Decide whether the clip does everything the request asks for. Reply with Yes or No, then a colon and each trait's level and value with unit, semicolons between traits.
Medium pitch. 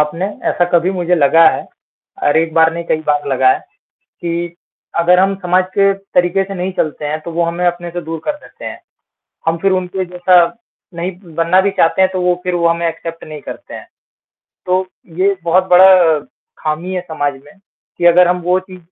Yes: medium, 175 Hz